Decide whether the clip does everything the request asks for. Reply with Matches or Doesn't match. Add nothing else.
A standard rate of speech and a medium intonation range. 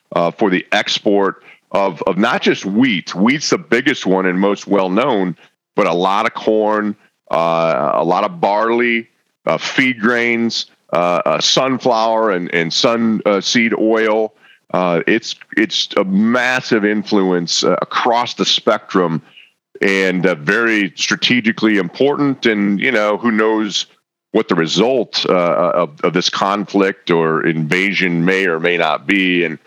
Matches